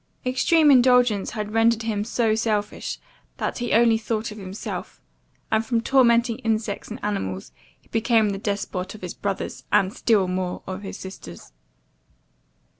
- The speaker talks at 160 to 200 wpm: No, average, 150 wpm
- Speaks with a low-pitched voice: No, high, 215 Hz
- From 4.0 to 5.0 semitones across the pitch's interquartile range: No, narrow, 2.6 semitones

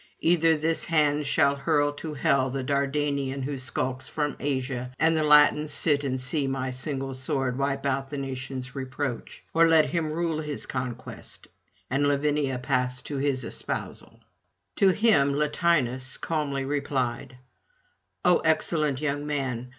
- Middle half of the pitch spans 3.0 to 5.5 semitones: No, narrow, 2.4 semitones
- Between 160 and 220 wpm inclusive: No, average, 145 wpm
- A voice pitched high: No, medium, 140 Hz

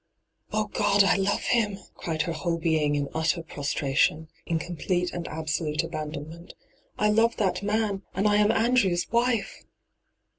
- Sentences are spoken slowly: No, average, 170 wpm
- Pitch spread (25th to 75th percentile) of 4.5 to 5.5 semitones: Yes, average, 4.8 semitones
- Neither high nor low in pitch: Yes, medium, 175 Hz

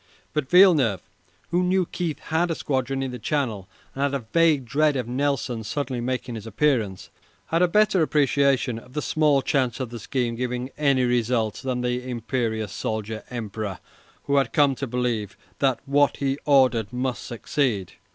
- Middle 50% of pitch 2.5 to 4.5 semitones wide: Yes, average, 3.5 semitones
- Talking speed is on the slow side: No, average, 170 wpm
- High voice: No, low, 130 Hz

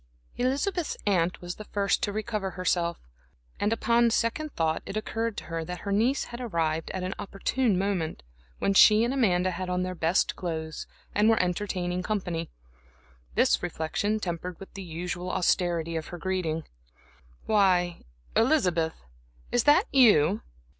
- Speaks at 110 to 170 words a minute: Yes, average, 150 wpm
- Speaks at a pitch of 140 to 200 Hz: Yes, medium, 185 Hz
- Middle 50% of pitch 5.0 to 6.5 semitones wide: No, average, 4.0 semitones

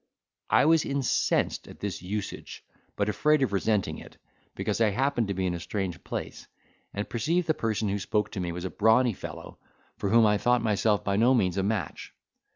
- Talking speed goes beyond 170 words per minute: Yes, average, 200 wpm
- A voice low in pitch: Yes, low, 105 Hz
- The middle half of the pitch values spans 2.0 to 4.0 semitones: Yes, average, 3.6 semitones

